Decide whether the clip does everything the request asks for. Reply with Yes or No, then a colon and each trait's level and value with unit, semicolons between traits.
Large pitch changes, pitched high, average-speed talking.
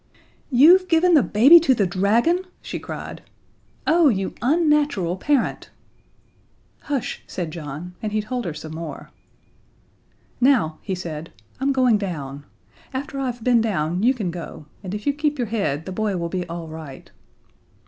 Yes: wide, 8.2 semitones; high, 210 Hz; average, 160 wpm